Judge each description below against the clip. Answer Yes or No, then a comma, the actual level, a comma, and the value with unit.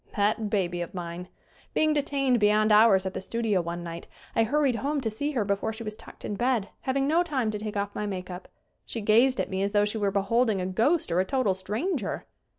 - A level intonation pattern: No, average, 4.6 semitones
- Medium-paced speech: No, fast, 235 wpm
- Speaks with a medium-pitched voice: No, high, 215 Hz